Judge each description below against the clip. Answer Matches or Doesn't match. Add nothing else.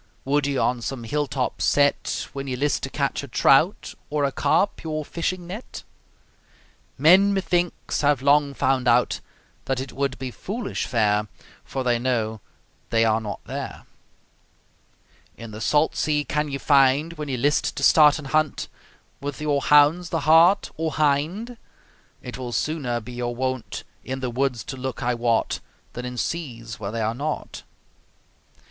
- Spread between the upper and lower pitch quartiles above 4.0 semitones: Doesn't match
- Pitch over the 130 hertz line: Matches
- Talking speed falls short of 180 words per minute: Matches